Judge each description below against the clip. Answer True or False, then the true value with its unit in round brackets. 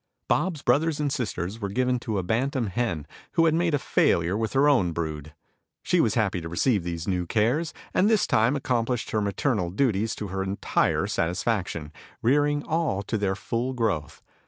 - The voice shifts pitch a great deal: True (6.5 semitones)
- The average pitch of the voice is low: True (110 Hz)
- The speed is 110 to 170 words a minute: False (180 wpm)